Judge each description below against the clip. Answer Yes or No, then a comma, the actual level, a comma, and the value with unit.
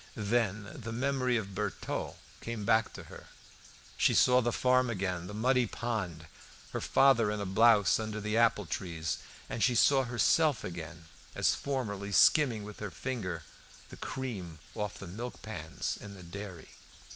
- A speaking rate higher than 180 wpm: No, average, 165 wpm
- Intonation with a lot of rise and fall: No, average, 3.9 semitones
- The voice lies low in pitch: Yes, low, 110 Hz